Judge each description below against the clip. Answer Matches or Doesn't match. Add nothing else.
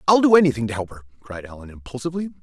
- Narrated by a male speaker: Matches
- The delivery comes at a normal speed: Doesn't match